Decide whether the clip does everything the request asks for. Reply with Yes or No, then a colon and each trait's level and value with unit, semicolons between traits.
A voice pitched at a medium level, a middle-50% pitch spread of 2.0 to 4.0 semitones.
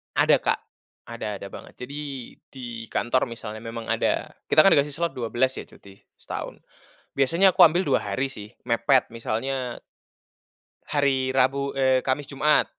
No: low, 130 Hz; average, 3.2 semitones